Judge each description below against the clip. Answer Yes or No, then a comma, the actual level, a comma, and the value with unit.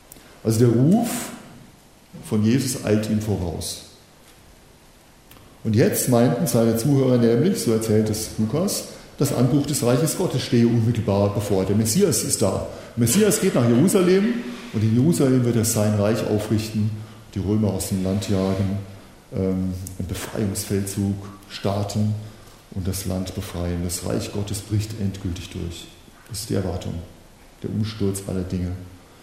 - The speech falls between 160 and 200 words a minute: No, average, 145 wpm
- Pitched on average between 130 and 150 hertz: No, low, 105 Hz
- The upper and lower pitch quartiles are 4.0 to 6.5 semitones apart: No, average, 3.6 semitones